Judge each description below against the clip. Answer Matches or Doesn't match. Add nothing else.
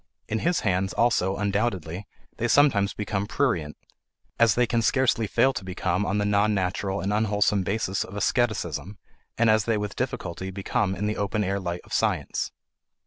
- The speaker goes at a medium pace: Matches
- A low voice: Matches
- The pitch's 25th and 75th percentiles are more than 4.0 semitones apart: Doesn't match